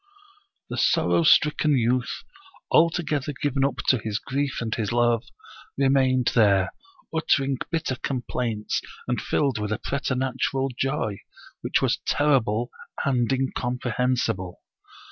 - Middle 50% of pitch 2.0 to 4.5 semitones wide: Yes, average, 3.0 semitones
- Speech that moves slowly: Yes, slow, 125 wpm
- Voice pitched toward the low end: Yes, low, 130 Hz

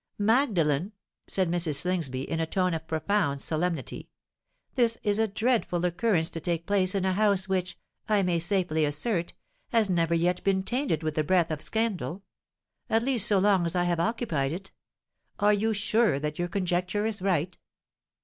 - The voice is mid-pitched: Yes, medium, 180 Hz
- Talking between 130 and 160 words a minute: No, average, 170 wpm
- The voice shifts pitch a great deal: No, average, 3.8 semitones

